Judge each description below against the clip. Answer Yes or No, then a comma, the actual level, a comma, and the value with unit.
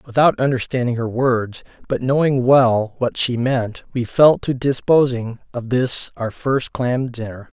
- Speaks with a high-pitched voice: No, low, 125 Hz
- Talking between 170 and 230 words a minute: No, average, 160 wpm